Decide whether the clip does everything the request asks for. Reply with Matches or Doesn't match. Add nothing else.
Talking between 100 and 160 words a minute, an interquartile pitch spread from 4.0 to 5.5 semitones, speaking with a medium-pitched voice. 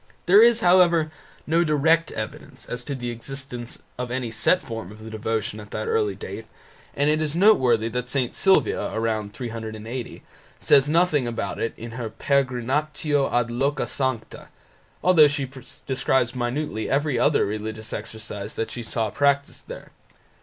Doesn't match